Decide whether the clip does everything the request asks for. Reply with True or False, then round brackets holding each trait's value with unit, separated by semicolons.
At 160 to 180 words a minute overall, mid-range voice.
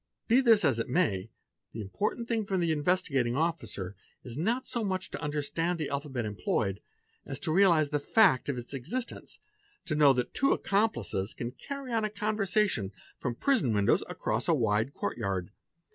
True (175 wpm; 155 Hz)